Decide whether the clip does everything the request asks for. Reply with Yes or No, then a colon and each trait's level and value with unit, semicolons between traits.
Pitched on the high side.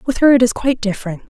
Yes: high, 230 Hz